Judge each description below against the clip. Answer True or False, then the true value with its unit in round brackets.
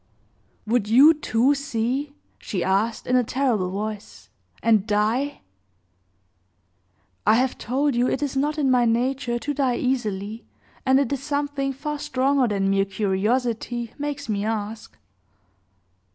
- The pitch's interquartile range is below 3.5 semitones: False (4.2 semitones)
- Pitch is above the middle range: True (245 Hz)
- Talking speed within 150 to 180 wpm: False (135 wpm)